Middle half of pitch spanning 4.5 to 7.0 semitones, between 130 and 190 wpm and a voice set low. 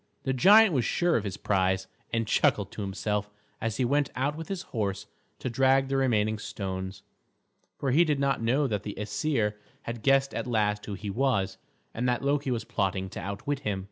No: average, 4.9 semitones; average, 200 wpm; low, 115 Hz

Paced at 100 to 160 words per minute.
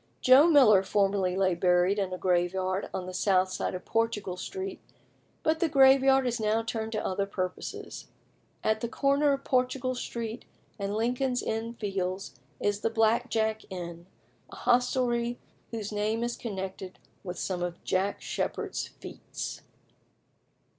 Yes: average, 145 wpm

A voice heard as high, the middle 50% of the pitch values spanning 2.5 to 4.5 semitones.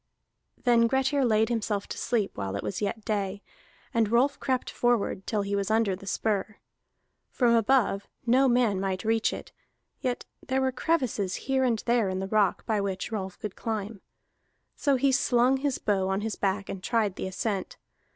Yes: high, 220 Hz; average, 3.6 semitones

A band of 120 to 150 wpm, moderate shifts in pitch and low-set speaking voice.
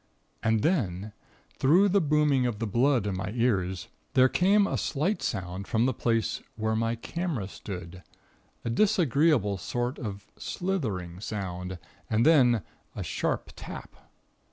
No: average, 140 wpm; wide, 6.9 semitones; low, 115 Hz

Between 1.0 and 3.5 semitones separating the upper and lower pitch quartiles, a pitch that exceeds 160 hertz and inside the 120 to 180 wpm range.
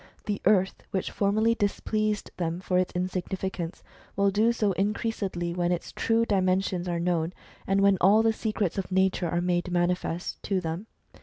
Yes: narrow, 2.6 semitones; high, 190 Hz; average, 165 wpm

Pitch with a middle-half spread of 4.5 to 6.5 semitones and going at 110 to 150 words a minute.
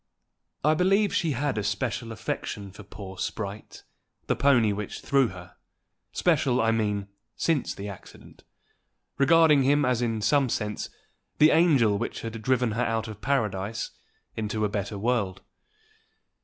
Yes: average, 5.1 semitones; average, 145 wpm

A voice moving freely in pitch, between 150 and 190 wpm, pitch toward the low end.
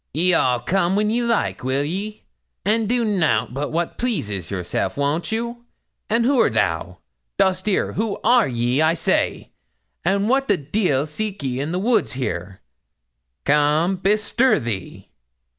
No: wide, 8.2 semitones; average, 155 wpm; medium, 175 Hz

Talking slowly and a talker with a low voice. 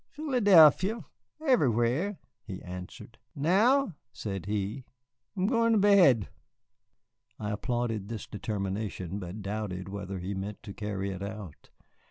Yes: slow, 115 wpm; low, 110 Hz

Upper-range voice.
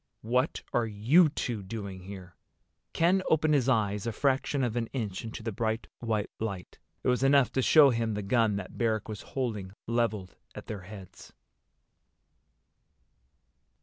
No: low, 115 Hz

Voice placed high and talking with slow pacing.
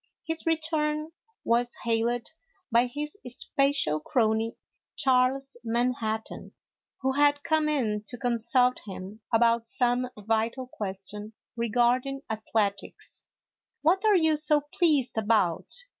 Yes: high, 245 Hz; slow, 115 wpm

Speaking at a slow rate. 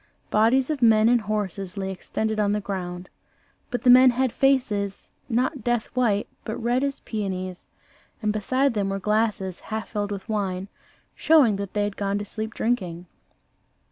No: average, 170 wpm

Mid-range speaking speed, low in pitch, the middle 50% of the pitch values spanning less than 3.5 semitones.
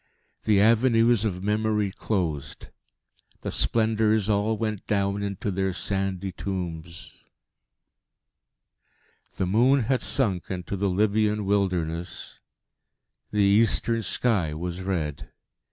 No: slow, 105 wpm; low, 100 Hz; average, 3.0 semitones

